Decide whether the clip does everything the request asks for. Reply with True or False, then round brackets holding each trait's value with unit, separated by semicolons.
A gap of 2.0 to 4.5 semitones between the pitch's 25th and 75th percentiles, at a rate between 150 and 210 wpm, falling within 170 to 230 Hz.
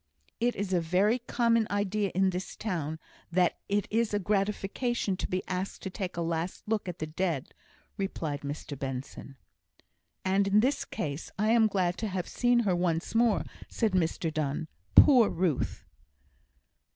True (4.2 semitones; 165 wpm; 190 Hz)